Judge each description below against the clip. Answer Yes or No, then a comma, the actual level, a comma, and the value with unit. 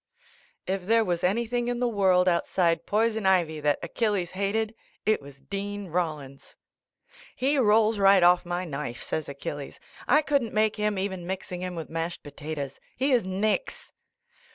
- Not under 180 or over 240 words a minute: No, average, 165 wpm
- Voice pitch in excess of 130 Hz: Yes, high, 190 Hz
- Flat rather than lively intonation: No, average, 4.5 semitones